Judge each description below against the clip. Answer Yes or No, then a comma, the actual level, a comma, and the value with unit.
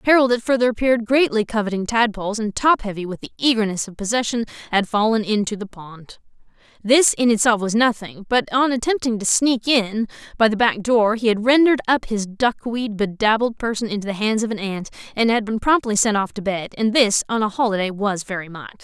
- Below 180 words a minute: No, fast, 205 wpm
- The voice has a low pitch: No, high, 220 Hz